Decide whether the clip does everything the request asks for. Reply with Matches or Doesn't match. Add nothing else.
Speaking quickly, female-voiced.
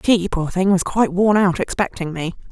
Matches